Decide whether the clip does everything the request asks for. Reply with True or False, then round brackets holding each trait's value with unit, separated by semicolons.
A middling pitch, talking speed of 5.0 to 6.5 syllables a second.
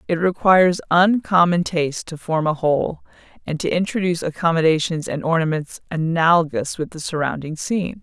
True (165 Hz; 5.5 syllables/s)